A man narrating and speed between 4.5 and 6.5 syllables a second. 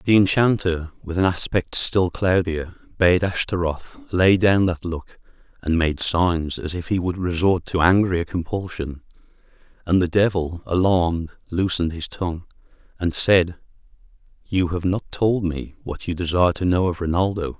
Yes: male; 4.6 syllables/s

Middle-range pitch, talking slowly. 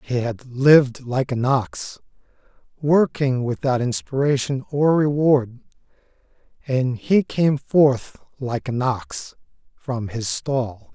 No: low, 130 Hz; slow, 115 wpm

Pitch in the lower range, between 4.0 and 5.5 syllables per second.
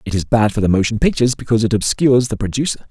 No: low, 115 Hz; 7.6 syllables/s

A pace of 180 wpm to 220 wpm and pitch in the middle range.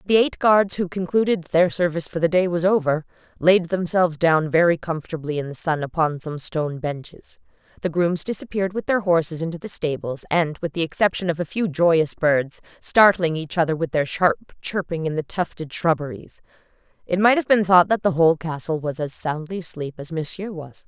Yes: average, 200 wpm; medium, 170 Hz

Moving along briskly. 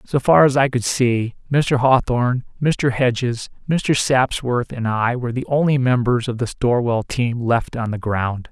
No: average, 185 wpm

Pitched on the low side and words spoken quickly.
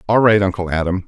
Yes: very low, 95 Hz; fast, 225 wpm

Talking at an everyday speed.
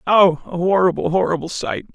Yes: average, 155 wpm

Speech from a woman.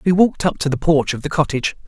No: male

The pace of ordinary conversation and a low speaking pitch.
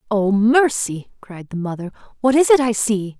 No: average, 190 wpm; high, 220 Hz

